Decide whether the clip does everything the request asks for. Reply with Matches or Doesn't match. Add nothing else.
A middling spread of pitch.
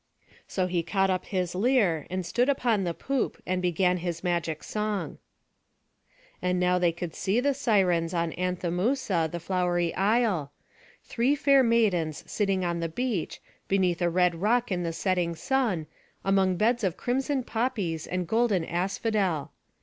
Matches